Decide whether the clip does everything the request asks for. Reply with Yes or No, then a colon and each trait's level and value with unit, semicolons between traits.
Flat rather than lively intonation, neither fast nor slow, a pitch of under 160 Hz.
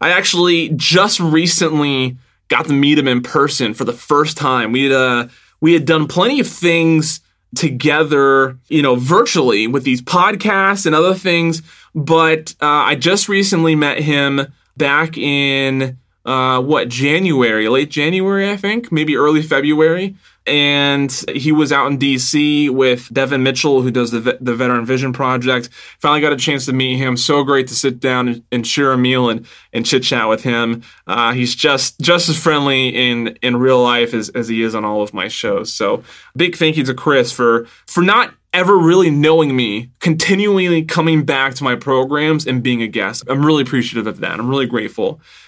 No: average, 4.2 semitones; average, 185 wpm; medium, 140 Hz